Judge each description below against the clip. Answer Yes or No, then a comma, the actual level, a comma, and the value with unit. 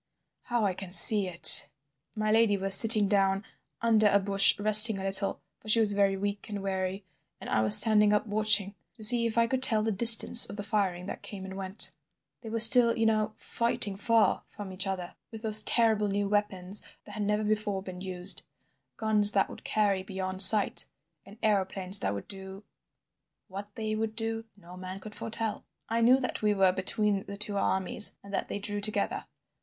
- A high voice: Yes, high, 205 Hz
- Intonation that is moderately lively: No, narrow, 2.0 semitones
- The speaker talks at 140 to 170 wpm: No, average, 195 wpm